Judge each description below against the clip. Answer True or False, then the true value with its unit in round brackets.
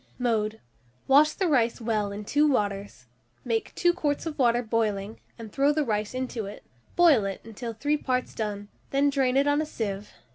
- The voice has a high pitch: True (235 Hz)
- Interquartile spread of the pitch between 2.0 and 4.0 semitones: False (5.2 semitones)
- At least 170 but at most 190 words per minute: True (185 wpm)